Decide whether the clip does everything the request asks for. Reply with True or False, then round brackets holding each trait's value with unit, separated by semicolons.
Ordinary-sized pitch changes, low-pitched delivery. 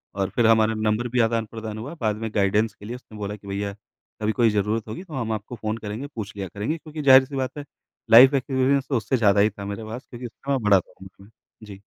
True (3.6 semitones; 110 Hz)